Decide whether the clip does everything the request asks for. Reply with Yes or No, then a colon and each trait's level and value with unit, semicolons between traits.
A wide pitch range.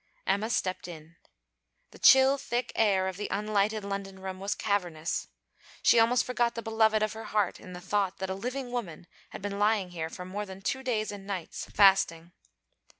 No: average, 2.8 semitones